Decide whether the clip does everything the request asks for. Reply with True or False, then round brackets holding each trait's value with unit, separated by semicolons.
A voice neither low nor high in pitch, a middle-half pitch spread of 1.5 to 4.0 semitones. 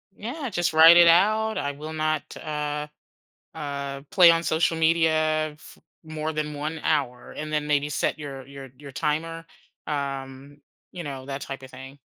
True (155 Hz; 2.4 semitones)